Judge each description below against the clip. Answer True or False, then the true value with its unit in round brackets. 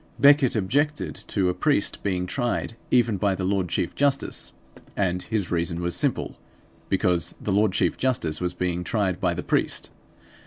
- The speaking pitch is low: True (95 Hz)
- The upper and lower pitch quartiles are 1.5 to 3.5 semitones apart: False (4.5 semitones)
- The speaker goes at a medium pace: True (165 wpm)